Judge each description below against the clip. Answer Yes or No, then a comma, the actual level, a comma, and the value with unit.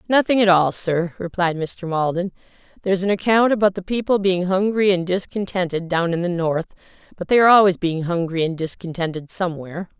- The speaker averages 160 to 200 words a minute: Yes, average, 180 wpm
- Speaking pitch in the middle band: Yes, medium, 180 Hz